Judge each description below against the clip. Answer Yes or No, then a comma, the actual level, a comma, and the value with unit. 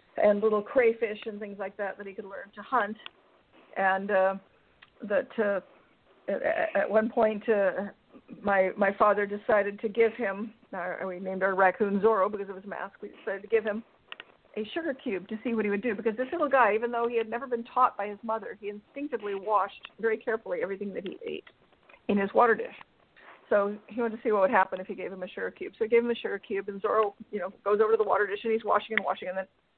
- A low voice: No, high, 210 Hz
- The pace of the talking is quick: Yes, fast, 240 wpm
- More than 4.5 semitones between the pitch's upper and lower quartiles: No, narrow, 2.5 semitones